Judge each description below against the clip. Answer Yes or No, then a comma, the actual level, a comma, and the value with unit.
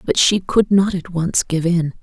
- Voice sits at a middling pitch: Yes, medium, 175 Hz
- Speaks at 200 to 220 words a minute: No, fast, 235 wpm